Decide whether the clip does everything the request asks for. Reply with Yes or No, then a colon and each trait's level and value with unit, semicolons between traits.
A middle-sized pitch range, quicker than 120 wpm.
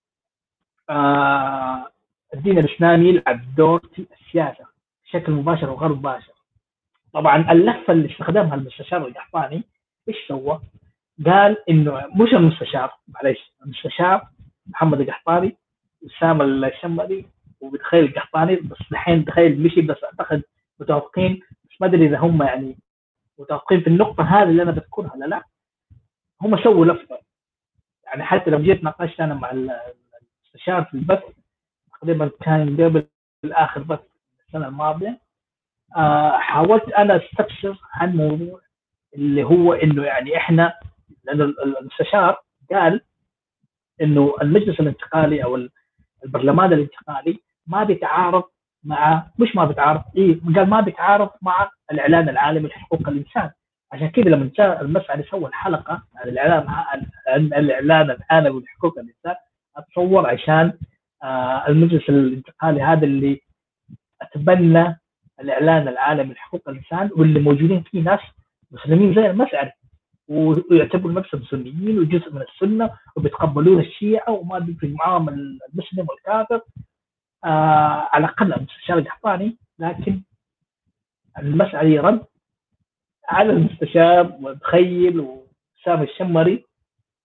No: average, 3.9 semitones; average, 115 wpm